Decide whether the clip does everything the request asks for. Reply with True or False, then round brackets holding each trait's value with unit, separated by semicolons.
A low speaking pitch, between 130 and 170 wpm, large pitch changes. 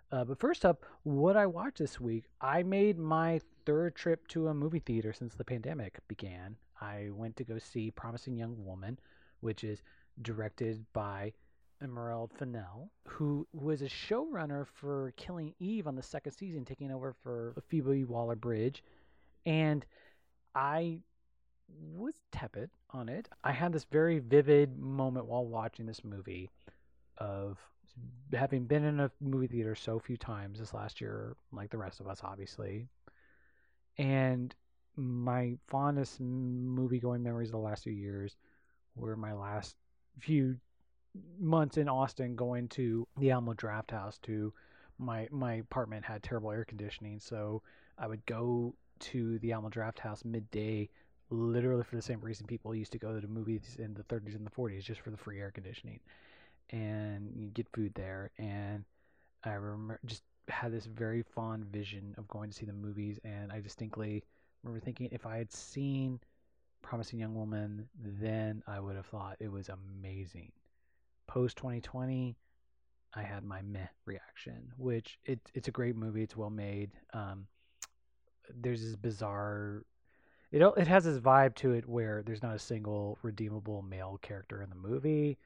False (115 Hz; 165 wpm; 3.7 semitones)